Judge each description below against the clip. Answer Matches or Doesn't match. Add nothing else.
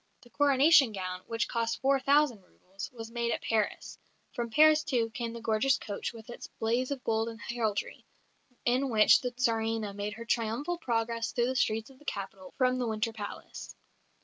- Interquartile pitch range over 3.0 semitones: Doesn't match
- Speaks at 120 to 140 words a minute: Doesn't match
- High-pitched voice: Matches